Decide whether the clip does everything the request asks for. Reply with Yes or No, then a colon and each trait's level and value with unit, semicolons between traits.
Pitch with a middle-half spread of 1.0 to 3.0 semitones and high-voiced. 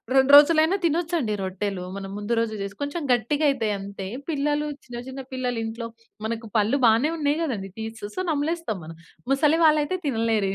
No: wide, 5.5 semitones; high, 245 Hz